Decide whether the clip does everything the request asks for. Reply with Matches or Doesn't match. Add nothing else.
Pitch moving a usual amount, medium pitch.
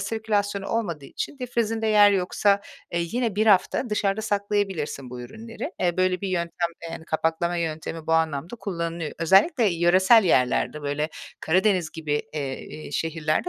Matches